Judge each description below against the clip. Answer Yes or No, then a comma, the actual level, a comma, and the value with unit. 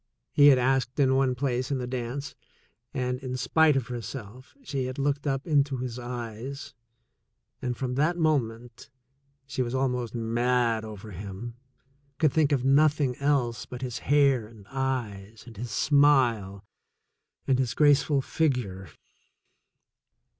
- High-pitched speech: No, low, 130 Hz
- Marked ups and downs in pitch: No, average, 2.9 semitones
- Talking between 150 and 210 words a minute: No, average, 140 wpm